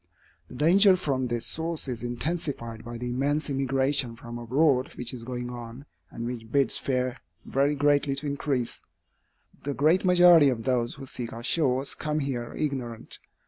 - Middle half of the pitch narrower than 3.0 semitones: No, average, 3.3 semitones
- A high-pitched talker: No, low, 135 Hz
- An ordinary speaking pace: Yes, average, 165 wpm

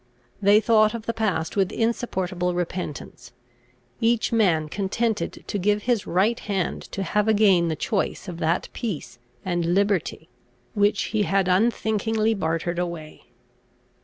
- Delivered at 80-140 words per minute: Yes, slow, 135 wpm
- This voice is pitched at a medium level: No, high, 195 Hz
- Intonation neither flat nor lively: Yes, average, 3.8 semitones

